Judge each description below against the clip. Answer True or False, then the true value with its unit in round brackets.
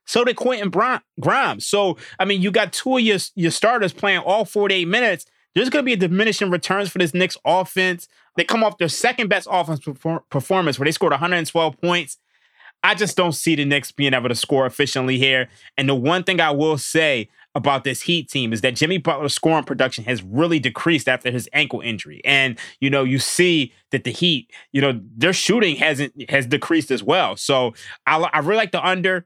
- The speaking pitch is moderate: True (165 Hz)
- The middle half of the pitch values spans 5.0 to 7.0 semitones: True (5.3 semitones)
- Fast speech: True (220 wpm)